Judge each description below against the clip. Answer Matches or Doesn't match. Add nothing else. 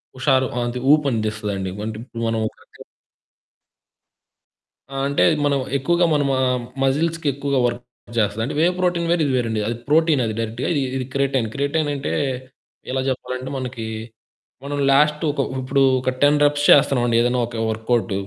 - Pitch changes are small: Doesn't match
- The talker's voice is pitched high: Doesn't match